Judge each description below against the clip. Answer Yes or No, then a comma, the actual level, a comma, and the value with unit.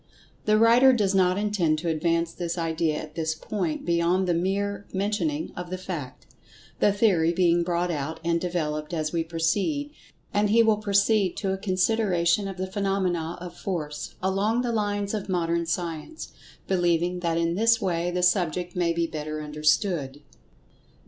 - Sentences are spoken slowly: No, average, 160 wpm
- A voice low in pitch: No, medium, 180 Hz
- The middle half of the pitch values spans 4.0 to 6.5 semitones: No, average, 3.3 semitones